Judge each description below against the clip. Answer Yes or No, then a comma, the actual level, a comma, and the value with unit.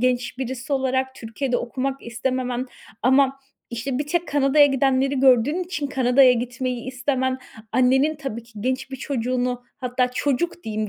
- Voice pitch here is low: No, very high, 260 Hz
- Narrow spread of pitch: Yes, narrow, 1.6 semitones